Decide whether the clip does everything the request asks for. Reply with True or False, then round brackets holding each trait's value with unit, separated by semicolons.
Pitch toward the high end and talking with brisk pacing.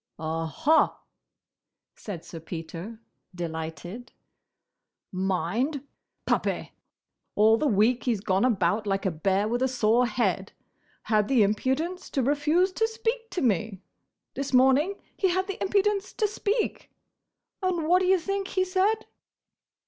False (250 Hz; 135 wpm)